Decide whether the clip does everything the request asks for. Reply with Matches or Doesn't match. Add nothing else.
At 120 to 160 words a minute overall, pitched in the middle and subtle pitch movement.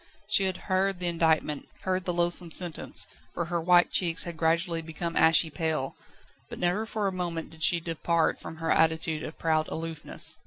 Doesn't match